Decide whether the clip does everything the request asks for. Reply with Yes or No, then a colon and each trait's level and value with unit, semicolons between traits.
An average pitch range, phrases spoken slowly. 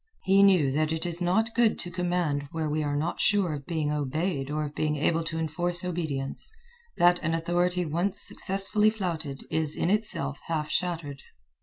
No: average, 3.1 semitones; average, 180 wpm